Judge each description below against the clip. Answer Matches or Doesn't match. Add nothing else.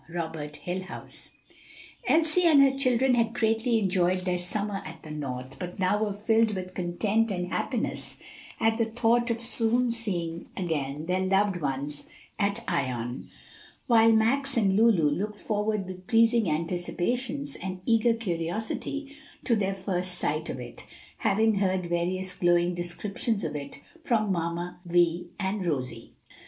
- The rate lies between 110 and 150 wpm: Matches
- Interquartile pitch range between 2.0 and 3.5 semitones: Doesn't match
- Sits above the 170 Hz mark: Matches